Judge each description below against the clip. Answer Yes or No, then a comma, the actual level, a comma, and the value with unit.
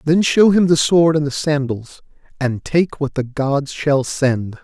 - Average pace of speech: Yes, average, 195 wpm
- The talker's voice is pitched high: No, medium, 145 Hz